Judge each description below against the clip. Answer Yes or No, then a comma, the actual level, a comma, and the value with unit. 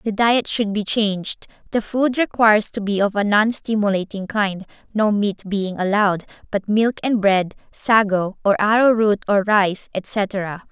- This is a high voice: Yes, high, 205 Hz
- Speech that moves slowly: No, average, 160 wpm